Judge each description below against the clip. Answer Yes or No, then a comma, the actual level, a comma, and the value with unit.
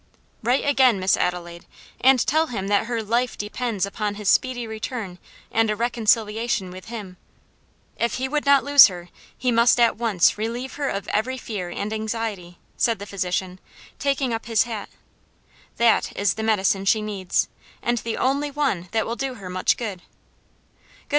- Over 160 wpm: Yes, average, 170 wpm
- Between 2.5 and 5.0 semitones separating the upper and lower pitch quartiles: Yes, average, 3.7 semitones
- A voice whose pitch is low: No, high, 220 Hz